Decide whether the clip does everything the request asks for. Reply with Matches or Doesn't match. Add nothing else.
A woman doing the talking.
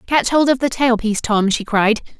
Matches